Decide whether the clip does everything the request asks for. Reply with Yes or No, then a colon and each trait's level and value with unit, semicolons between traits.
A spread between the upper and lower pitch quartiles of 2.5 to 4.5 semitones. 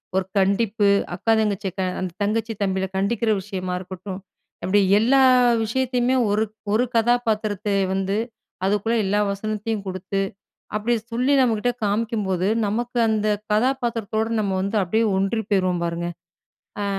Yes: average, 2.9 semitones